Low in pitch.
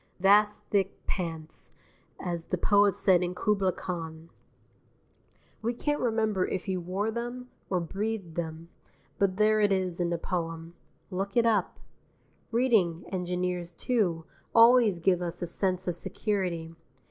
No: medium, 185 Hz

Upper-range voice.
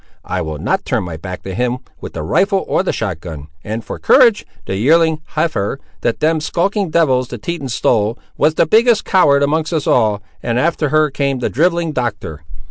No: medium, 140 Hz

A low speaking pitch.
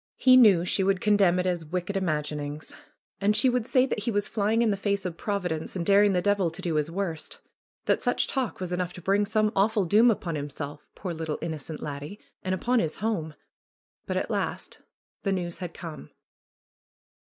No: medium, 185 Hz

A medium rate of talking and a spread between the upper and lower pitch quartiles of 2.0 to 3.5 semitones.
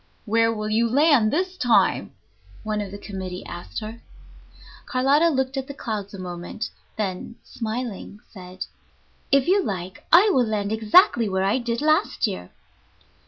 No: average, 155 wpm; average, 4.9 semitones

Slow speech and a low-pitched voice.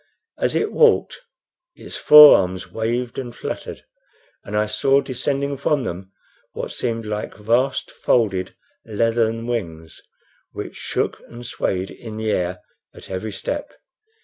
Yes: slow, 130 wpm; low, 115 Hz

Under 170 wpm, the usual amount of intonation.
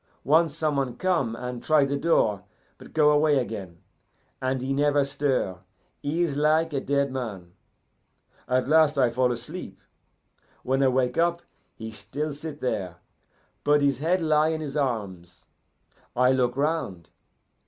Yes: average, 155 wpm; average, 3.9 semitones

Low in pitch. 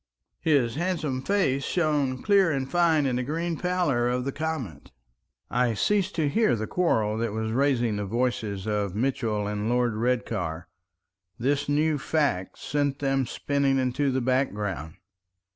Yes: low, 130 Hz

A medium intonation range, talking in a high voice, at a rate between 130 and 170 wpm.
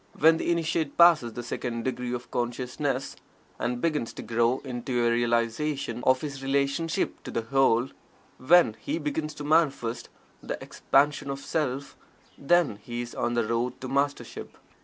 No: average, 3.7 semitones; low, 135 Hz; average, 160 wpm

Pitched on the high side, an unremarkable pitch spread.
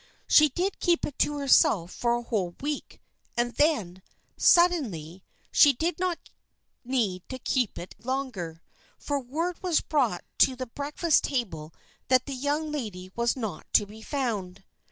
No: very high, 255 Hz; wide, 6.8 semitones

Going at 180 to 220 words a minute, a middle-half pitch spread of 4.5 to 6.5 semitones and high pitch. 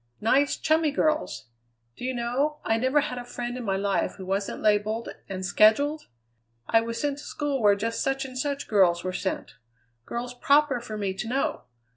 Yes: average, 190 wpm; average, 5.0 semitones; high, 240 Hz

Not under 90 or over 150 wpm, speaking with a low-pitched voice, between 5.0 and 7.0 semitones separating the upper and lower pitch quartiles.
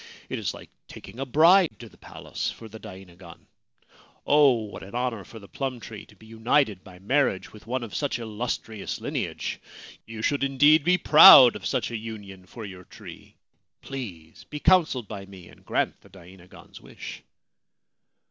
No: average, 175 wpm; low, 115 Hz; wide, 5.6 semitones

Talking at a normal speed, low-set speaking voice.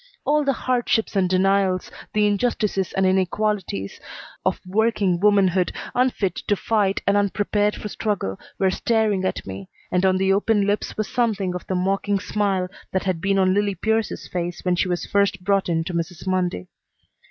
No: average, 175 wpm; high, 195 Hz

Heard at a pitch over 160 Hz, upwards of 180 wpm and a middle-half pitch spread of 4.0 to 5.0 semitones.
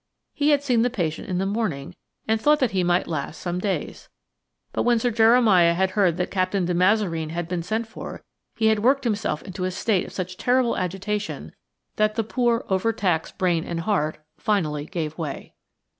Yes: high, 190 Hz; average, 190 wpm; average, 4.3 semitones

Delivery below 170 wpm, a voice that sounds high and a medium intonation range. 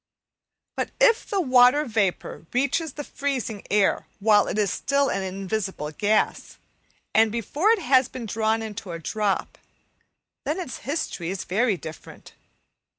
No: average, 145 wpm; high, 220 Hz; wide, 5.8 semitones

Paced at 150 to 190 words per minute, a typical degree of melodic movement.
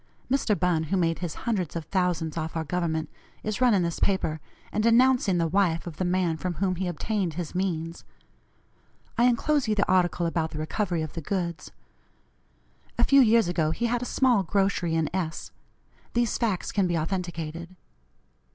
Yes: average, 180 wpm; average, 3.8 semitones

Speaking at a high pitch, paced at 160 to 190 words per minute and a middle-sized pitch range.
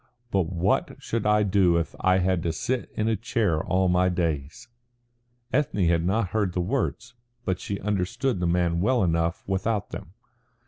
No: very low, 95 Hz; average, 175 wpm; average, 3.6 semitones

